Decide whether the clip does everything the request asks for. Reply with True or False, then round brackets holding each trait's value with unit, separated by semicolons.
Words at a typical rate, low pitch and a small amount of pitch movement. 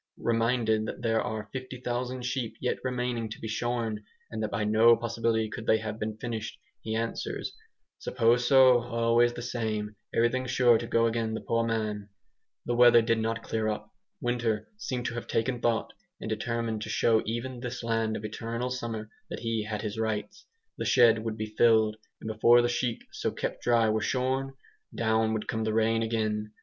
True (185 wpm; 115 Hz; 1.6 semitones)